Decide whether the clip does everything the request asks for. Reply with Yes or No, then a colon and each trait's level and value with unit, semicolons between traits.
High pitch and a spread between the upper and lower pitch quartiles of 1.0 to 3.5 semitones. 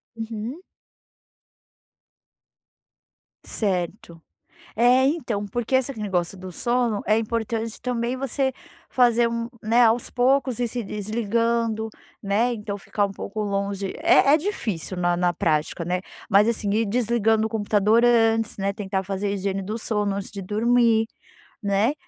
Yes: high, 220 Hz; average, 3.0 semitones